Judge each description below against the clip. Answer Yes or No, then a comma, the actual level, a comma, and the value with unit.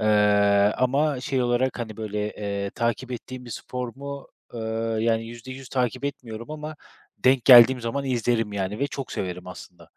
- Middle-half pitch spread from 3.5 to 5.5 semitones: No, average, 3.0 semitones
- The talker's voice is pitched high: No, low, 120 Hz